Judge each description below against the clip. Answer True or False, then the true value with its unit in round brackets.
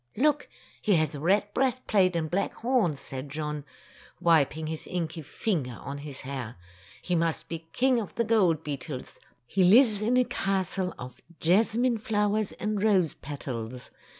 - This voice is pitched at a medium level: True (175 Hz)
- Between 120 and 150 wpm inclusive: False (160 wpm)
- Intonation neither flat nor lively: False (6.2 semitones)